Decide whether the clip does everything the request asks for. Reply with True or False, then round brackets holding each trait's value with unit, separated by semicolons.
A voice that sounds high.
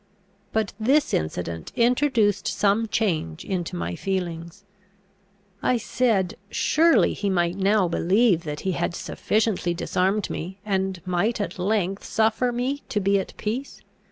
True (195 Hz)